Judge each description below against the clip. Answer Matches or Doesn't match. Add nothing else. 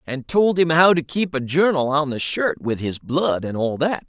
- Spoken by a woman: Doesn't match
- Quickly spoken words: Matches